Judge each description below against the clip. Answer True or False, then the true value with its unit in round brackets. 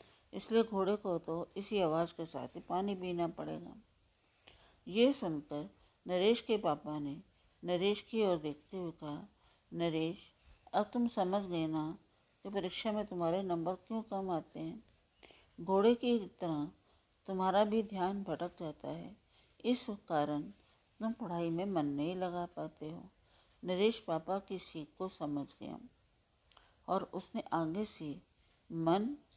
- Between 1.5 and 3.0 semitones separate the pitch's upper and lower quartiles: False (4.2 semitones)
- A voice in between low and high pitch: True (180 Hz)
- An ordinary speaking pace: True (145 wpm)